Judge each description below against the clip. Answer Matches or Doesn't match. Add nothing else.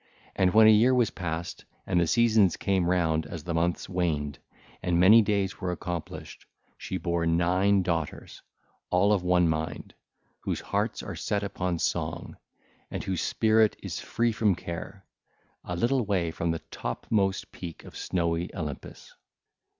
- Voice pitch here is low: Matches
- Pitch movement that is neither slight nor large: Matches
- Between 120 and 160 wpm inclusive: Matches